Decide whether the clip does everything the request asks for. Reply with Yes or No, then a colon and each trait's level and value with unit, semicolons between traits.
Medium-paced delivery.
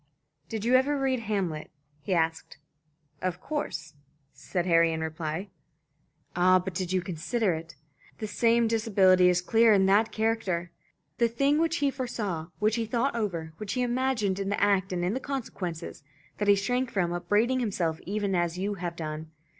Yes: average, 175 wpm